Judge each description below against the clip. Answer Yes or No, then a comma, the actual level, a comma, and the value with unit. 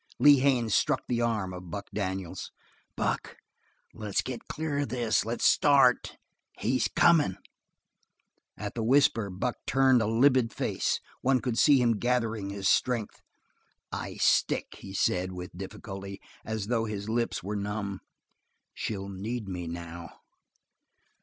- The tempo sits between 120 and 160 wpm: Yes, average, 140 wpm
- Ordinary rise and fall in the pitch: Yes, average, 4.1 semitones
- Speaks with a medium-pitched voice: No, low, 110 Hz